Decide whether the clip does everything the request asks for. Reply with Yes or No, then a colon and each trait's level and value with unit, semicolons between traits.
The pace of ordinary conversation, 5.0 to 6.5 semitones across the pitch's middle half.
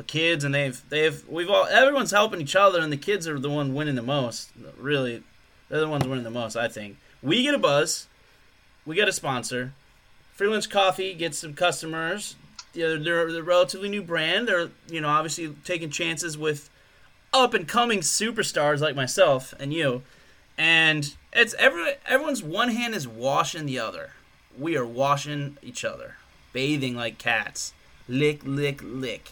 Yes: average, 170 wpm; wide, 5.4 semitones